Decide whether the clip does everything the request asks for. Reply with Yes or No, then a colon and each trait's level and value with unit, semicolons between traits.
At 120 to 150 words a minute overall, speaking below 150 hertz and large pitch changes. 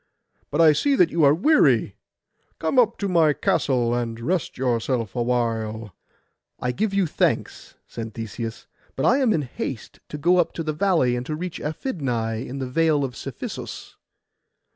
No: average, 165 wpm; medium, 140 Hz; wide, 6.3 semitones